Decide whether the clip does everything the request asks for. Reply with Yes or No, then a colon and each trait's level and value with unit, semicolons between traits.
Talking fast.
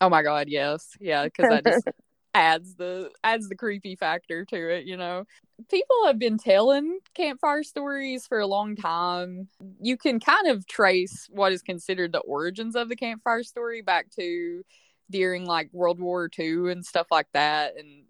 No: average, 180 wpm